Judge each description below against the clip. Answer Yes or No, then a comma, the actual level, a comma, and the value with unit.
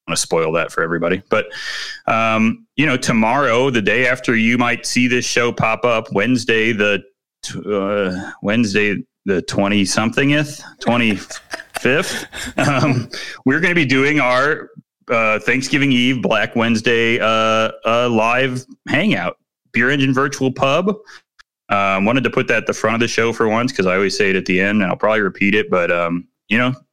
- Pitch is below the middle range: Yes, low, 120 Hz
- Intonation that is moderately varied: Yes, average, 3.6 semitones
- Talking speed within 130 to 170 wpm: No, average, 180 wpm